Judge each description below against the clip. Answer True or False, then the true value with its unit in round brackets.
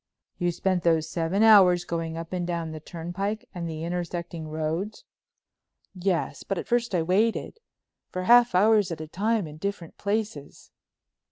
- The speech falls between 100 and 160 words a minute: True (155 wpm)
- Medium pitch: True (175 Hz)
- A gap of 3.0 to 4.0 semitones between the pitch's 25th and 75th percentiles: True (3.5 semitones)